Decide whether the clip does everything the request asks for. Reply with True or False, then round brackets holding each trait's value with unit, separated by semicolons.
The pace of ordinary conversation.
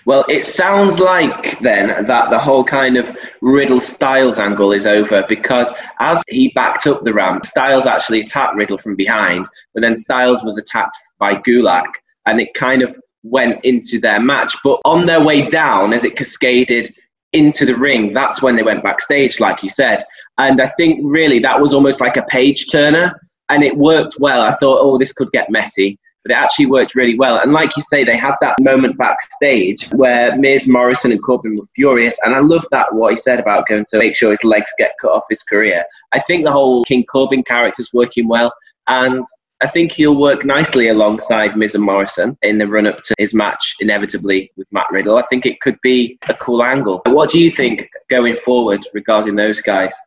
False (210 wpm)